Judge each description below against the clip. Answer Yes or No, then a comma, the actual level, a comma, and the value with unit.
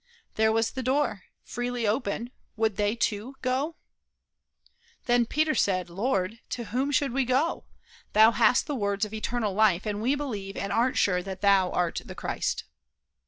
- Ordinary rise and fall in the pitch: Yes, average, 4.0 semitones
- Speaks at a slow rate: No, average, 165 wpm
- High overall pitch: Yes, high, 225 Hz